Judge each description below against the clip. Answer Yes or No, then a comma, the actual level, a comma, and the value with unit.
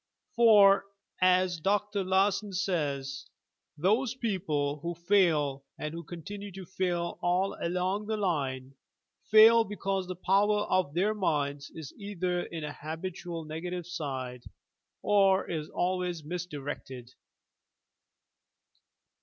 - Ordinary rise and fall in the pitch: Yes, average, 4.3 semitones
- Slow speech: Yes, slow, 115 wpm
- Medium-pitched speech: Yes, medium, 180 Hz